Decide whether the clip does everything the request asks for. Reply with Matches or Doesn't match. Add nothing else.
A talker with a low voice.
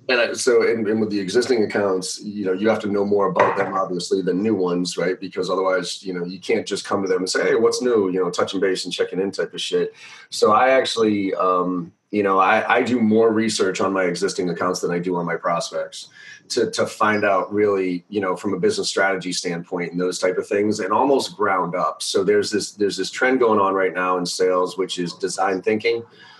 Matches